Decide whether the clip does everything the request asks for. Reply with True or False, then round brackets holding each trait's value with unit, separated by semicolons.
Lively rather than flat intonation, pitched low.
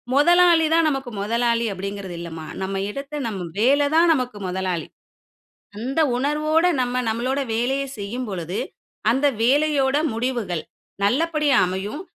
False (6.4 semitones; 250 Hz)